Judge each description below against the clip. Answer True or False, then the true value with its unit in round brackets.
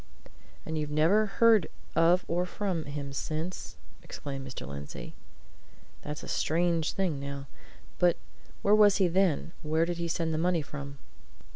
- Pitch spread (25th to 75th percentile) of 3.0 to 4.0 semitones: True (3.6 semitones)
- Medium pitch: True (165 Hz)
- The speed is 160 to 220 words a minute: False (150 wpm)